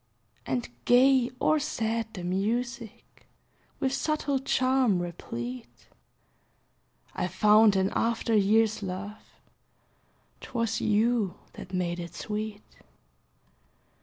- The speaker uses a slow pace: Yes, slow, 95 wpm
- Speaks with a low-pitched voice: No, high, 215 Hz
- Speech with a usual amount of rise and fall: Yes, average, 4.3 semitones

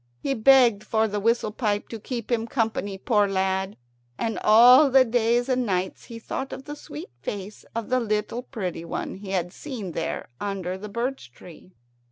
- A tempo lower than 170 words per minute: No, average, 185 wpm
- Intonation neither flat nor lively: Yes, average, 3.9 semitones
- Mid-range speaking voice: No, high, 220 Hz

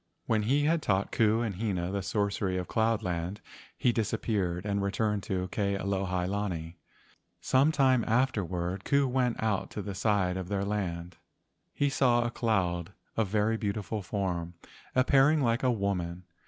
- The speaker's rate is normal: Yes, average, 160 wpm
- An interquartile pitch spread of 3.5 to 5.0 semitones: Yes, average, 3.8 semitones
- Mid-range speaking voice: No, low, 100 Hz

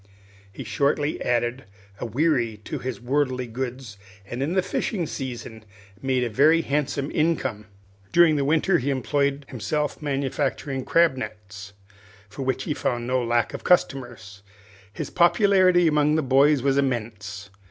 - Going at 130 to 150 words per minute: Yes, average, 145 wpm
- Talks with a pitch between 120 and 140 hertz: Yes, low, 135 Hz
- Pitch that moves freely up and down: No, average, 3.9 semitones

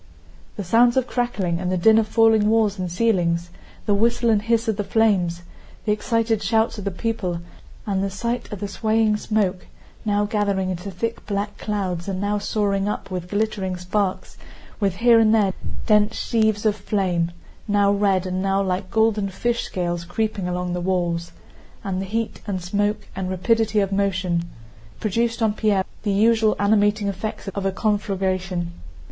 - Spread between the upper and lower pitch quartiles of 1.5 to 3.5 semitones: Yes, average, 2.8 semitones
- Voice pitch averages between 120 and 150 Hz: No, high, 205 Hz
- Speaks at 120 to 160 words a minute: No, average, 175 wpm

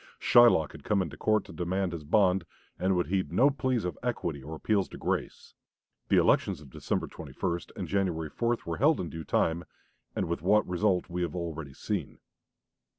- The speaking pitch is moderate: No, very low, 90 Hz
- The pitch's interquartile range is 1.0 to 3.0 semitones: No, average, 4.2 semitones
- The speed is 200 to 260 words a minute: No, average, 190 wpm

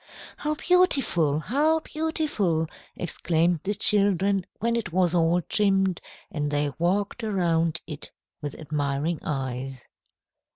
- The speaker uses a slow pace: Yes, slow, 115 wpm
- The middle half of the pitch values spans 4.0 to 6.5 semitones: Yes, average, 5.1 semitones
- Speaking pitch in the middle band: Yes, medium, 175 Hz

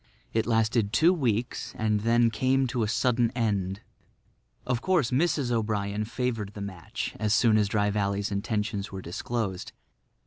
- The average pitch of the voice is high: No, low, 110 Hz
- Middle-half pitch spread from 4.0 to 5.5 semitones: No, average, 2.9 semitones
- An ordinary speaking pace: Yes, average, 150 wpm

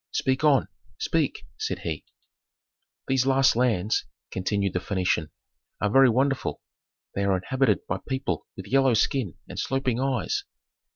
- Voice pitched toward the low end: Yes, low, 120 Hz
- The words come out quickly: No, slow, 135 wpm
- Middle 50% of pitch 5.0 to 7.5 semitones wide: Yes, wide, 5.6 semitones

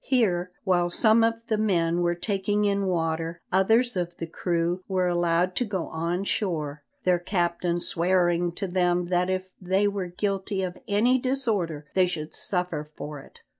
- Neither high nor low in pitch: Yes, medium, 180 Hz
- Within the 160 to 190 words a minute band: Yes, average, 170 wpm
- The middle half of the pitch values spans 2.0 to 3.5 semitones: Yes, narrow, 2.6 semitones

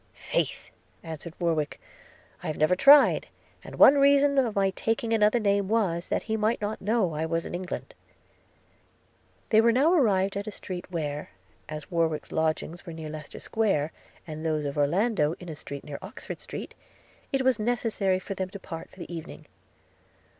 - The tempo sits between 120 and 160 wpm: No, average, 175 wpm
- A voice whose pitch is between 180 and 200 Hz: Yes, high, 190 Hz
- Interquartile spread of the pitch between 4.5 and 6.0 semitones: Yes, wide, 5.6 semitones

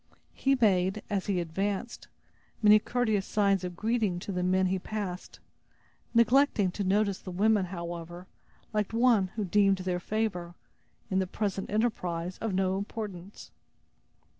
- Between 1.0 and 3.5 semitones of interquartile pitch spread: Yes, average, 2.8 semitones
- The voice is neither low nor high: No, high, 195 Hz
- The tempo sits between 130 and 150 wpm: Yes, average, 140 wpm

